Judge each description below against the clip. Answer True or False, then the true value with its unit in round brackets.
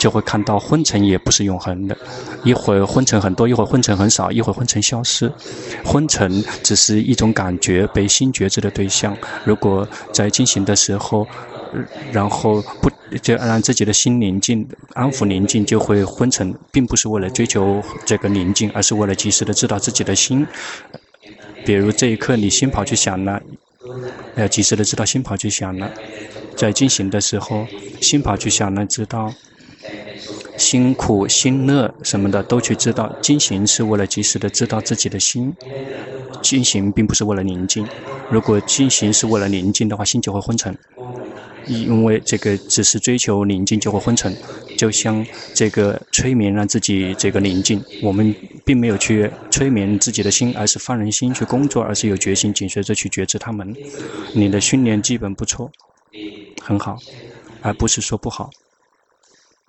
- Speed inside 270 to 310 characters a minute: False (260 characters per minute)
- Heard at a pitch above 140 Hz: False (105 Hz)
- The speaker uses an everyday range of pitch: True (3.1 semitones)